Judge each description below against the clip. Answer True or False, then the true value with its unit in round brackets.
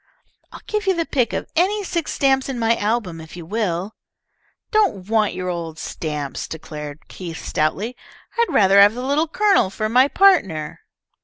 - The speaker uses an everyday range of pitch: False (8.9 semitones)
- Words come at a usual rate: True (170 wpm)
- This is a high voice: True (215 Hz)